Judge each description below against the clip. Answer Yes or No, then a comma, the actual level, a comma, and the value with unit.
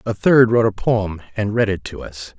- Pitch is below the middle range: Yes, low, 105 Hz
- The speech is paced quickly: Yes, fast, 250 wpm